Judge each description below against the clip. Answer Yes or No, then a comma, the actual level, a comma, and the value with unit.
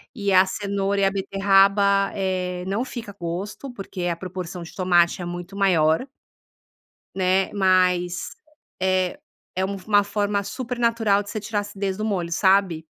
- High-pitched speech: Yes, high, 195 Hz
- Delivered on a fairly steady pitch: Yes, narrow, 1.8 semitones